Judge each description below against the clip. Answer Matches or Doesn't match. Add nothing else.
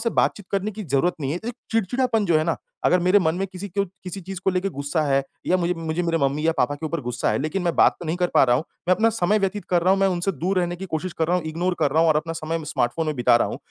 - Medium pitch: Matches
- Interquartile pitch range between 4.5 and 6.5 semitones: Doesn't match